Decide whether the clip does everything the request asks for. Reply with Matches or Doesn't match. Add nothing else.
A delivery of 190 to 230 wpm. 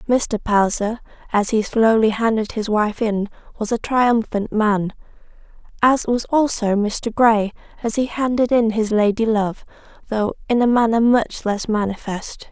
Doesn't match